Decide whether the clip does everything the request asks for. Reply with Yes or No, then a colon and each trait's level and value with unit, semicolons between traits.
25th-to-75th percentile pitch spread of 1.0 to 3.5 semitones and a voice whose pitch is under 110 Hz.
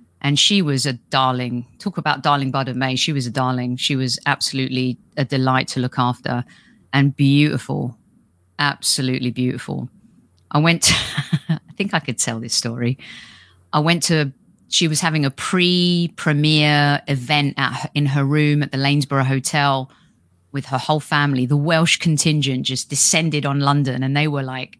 No: average, 2.7 semitones; medium, 140 Hz